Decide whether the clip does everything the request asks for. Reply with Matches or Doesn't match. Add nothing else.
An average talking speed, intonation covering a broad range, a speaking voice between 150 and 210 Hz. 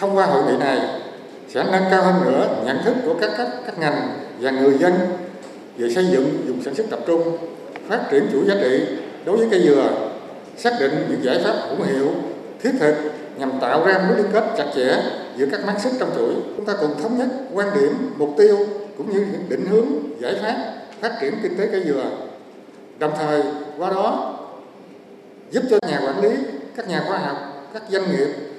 Matches